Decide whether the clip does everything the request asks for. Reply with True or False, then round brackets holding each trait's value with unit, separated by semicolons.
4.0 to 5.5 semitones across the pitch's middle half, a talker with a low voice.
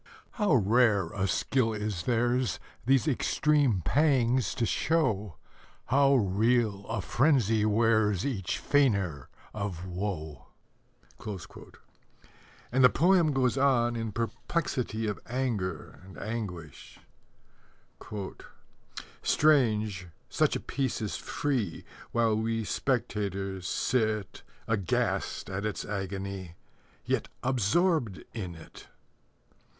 True (4.8 semitones; 110 Hz)